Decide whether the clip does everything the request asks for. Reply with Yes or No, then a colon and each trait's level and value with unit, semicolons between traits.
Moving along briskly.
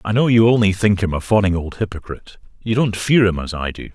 Yes: fast, 245 wpm